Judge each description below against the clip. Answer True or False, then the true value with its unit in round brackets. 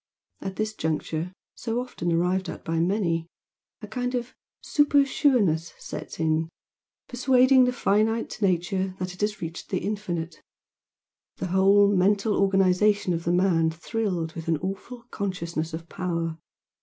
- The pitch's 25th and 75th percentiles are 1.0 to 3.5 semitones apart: False (4.3 semitones)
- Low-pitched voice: False (190 Hz)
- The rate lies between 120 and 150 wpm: True (145 wpm)